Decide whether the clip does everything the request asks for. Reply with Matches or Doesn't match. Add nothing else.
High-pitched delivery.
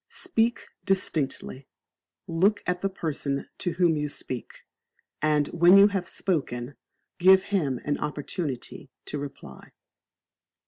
Doesn't match